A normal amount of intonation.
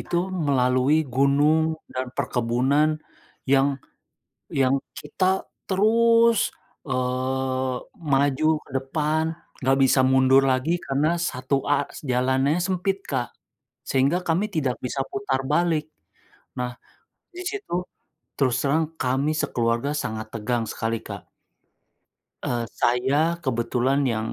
Yes: average, 3.7 semitones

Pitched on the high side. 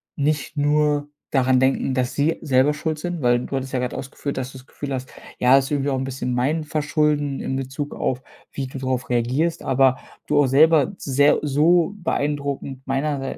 No: medium, 140 Hz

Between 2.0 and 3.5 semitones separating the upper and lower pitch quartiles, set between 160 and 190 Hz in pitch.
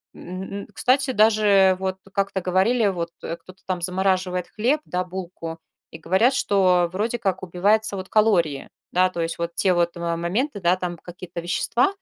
Yes: average, 2.8 semitones; medium, 185 Hz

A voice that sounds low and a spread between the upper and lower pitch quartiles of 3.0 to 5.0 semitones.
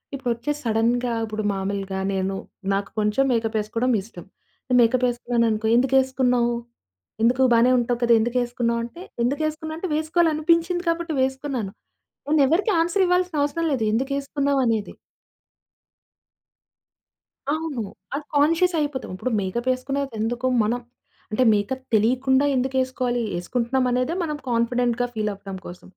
No: very high, 250 Hz; average, 3.8 semitones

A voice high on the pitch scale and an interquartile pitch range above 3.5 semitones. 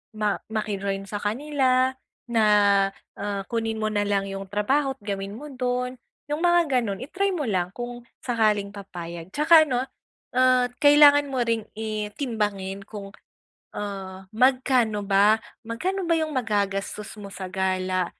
Yes: high, 220 Hz; average, 4.5 semitones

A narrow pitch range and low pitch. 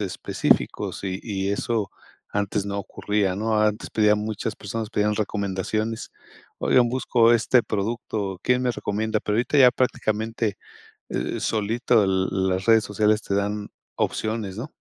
Yes: narrow, 2.0 semitones; low, 105 Hz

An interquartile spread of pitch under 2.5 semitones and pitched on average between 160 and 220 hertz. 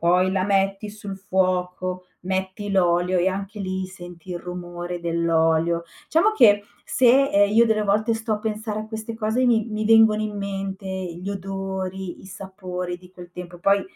No: average, 2.8 semitones; high, 190 Hz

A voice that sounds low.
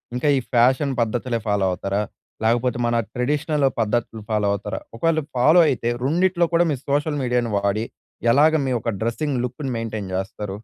Yes: low, 120 Hz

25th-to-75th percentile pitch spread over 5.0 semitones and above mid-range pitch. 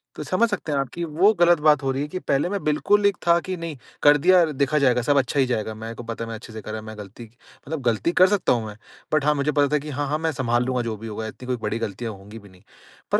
No: wide, 5.6 semitones; low, 135 Hz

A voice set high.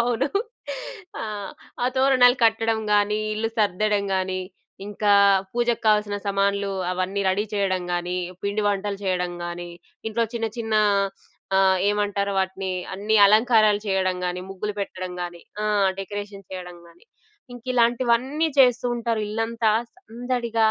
Yes: high, 205 Hz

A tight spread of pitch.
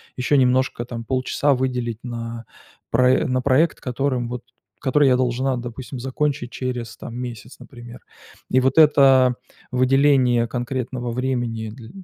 Yes: narrow, 1.7 semitones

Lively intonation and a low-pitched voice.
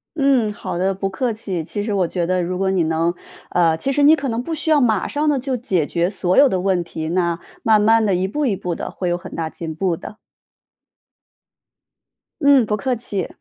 No: wide, 5.9 semitones; high, 195 Hz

